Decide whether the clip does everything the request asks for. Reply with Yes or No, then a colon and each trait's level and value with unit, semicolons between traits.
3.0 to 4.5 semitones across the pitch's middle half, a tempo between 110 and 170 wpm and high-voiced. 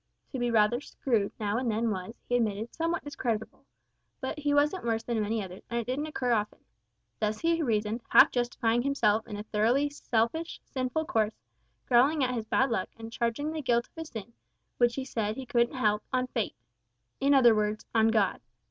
No: average, 3.5 semitones; average, 195 wpm; high, 235 Hz